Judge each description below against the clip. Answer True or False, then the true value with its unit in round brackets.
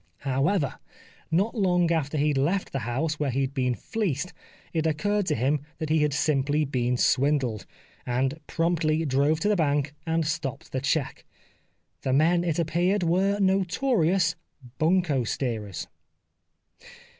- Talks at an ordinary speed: True (150 wpm)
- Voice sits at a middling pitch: True (155 Hz)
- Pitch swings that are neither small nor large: True (4.3 semitones)